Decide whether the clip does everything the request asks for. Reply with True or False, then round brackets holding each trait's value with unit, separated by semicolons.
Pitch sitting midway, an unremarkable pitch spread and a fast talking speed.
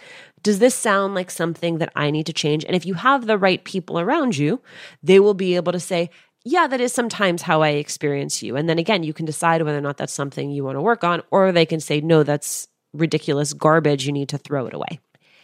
True (165 Hz; 4.4 semitones; 245 wpm)